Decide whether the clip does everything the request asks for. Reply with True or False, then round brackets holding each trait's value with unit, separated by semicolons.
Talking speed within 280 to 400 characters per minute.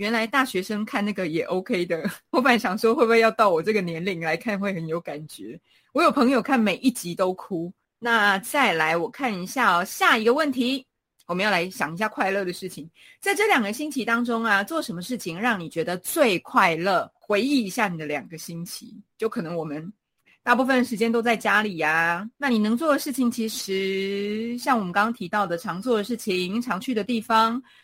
True (310 characters per minute)